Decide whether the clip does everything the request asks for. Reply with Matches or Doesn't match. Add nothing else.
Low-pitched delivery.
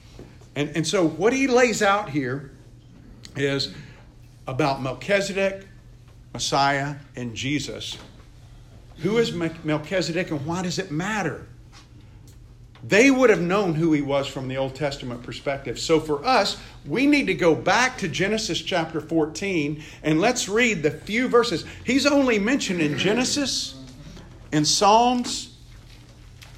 Doesn't match